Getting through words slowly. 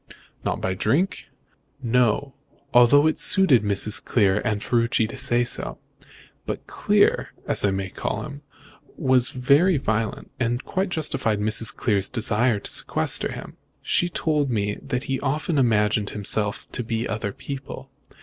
No: average, 150 wpm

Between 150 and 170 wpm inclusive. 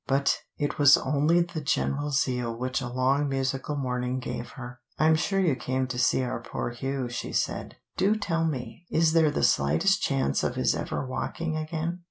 No: average, 190 wpm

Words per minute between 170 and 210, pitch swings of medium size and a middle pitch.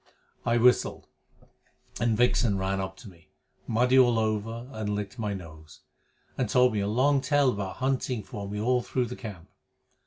No: average, 175 wpm; average, 3.8 semitones; low, 110 Hz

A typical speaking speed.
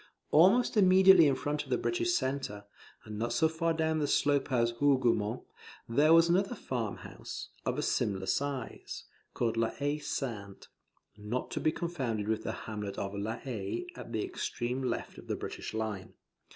Yes: average, 175 wpm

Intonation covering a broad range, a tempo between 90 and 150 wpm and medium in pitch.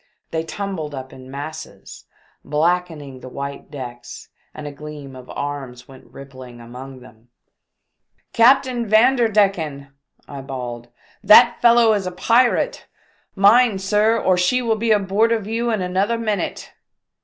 Yes: wide, 8.2 semitones; slow, 135 wpm; medium, 180 Hz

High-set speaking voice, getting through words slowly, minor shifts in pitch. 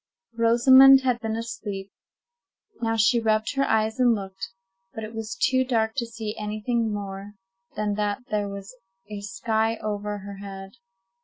No: high, 220 Hz; average, 160 wpm; narrow, 2.3 semitones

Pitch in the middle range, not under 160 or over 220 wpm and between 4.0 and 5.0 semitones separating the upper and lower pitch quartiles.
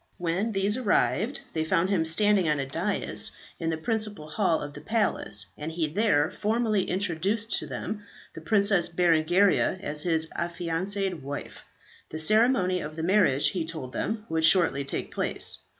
Yes: medium, 175 Hz; average, 165 wpm; average, 4.4 semitones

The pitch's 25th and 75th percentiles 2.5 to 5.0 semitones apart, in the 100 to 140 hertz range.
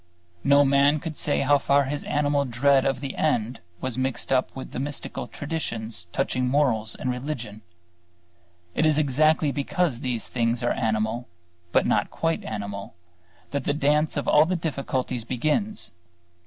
Yes: average, 3.5 semitones; low, 135 Hz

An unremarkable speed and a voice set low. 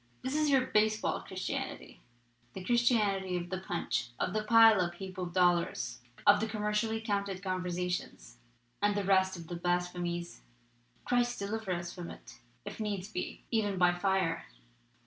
No: average, 165 wpm; high, 190 Hz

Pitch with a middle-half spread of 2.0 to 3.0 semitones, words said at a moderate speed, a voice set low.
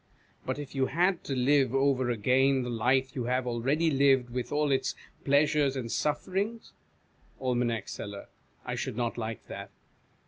Yes: narrow, 2.6 semitones; average, 160 wpm; low, 130 Hz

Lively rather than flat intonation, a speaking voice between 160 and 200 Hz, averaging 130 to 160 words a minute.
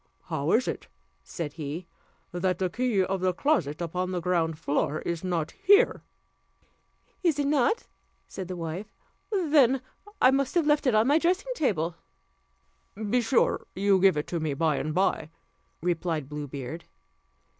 Yes: wide, 8.6 semitones; medium, 185 Hz; average, 155 wpm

